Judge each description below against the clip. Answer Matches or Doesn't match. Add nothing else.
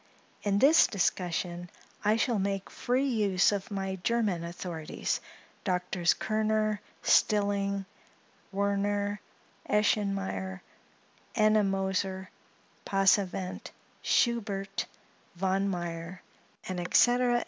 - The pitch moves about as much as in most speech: Doesn't match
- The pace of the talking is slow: Matches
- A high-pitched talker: Matches